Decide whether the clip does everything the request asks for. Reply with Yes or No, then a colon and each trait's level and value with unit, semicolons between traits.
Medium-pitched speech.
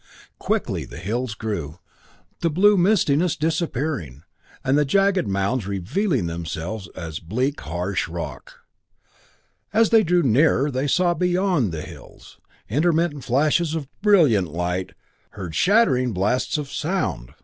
No: low, 130 Hz